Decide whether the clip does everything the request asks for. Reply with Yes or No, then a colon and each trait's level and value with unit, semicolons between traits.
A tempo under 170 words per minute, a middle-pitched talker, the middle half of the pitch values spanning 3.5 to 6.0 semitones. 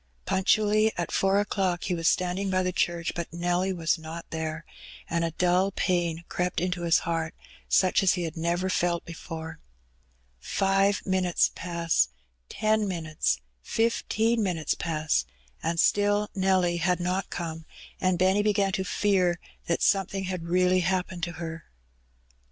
No: average, 155 wpm; medium, 180 Hz; narrow, 2.4 semitones